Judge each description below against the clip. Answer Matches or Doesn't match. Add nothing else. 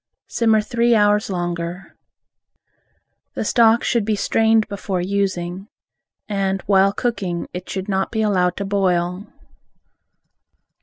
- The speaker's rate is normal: Doesn't match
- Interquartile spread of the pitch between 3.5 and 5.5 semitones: Doesn't match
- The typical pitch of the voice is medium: Doesn't match